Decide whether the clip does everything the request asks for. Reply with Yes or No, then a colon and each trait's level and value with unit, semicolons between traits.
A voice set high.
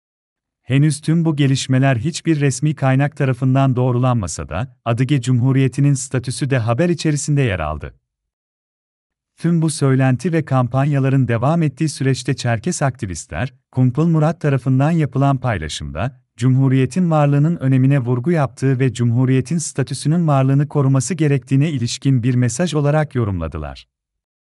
No: low, 135 Hz